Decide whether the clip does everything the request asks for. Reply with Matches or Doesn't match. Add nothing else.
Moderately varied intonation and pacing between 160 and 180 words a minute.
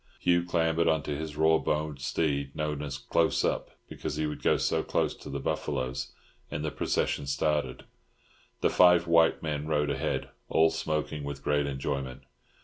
Doesn't match